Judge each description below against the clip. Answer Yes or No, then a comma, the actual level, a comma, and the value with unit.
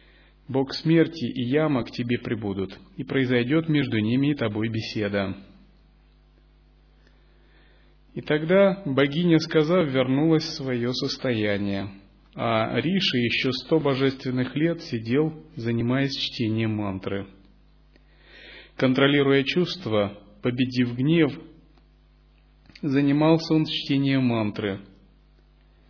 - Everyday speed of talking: No, slow, 95 wpm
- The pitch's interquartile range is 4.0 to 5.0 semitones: No, wide, 5.6 semitones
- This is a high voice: No, low, 130 Hz